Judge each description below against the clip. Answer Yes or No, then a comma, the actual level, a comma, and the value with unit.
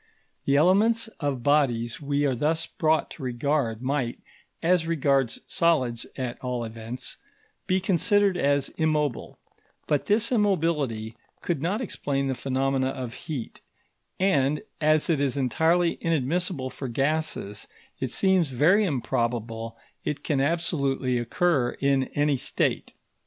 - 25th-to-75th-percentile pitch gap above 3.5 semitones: Yes, average, 4.5 semitones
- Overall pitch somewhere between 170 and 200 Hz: No, medium, 140 Hz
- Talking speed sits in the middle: No, slow, 130 wpm